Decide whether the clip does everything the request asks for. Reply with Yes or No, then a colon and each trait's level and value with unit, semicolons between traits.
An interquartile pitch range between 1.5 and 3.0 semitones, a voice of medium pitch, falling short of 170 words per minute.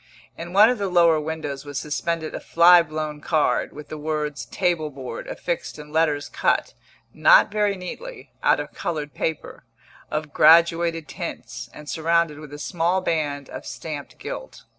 Yes: narrow, 2.5 semitones; medium, 160 Hz; average, 160 wpm